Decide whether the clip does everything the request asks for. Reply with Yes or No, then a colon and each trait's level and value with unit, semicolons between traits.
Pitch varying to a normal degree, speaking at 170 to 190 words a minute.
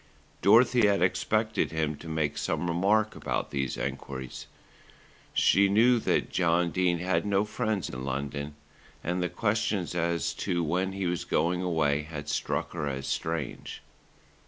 No: average, 4.6 semitones; average, 150 wpm